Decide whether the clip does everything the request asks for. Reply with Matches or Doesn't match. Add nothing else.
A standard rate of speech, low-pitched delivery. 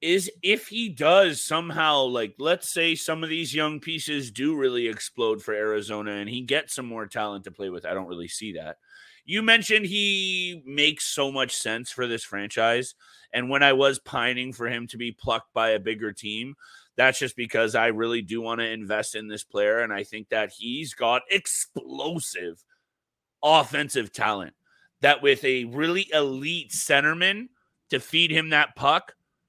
Doesn't match